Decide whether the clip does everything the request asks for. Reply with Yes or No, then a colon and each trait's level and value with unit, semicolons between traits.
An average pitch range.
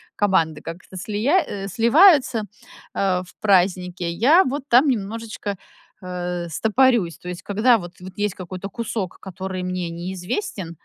Yes: average, 4.1 semitones